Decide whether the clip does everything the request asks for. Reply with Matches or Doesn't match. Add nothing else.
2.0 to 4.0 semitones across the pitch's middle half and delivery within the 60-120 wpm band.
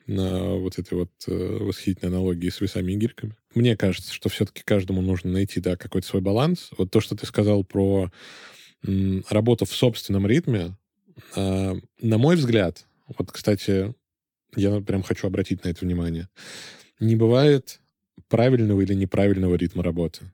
Doesn't match